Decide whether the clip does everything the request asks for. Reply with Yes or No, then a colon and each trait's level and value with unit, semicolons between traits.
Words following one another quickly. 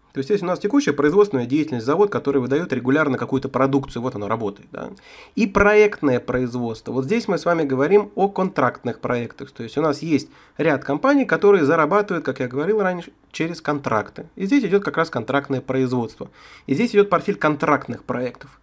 Yes: fast, 185 wpm